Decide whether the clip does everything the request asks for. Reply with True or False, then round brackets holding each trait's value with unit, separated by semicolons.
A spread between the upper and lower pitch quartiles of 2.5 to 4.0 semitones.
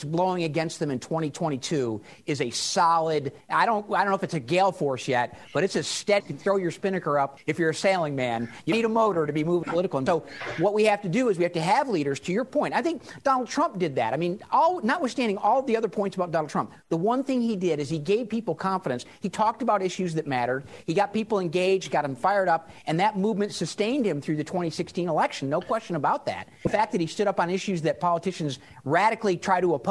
False (5.0 semitones)